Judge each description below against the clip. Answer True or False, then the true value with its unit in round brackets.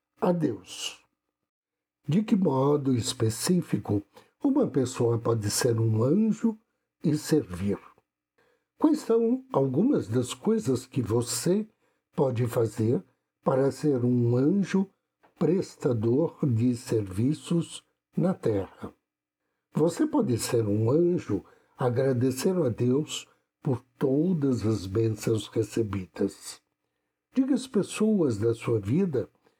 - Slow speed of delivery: True (105 wpm)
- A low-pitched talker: True (130 Hz)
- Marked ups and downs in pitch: True (7.4 semitones)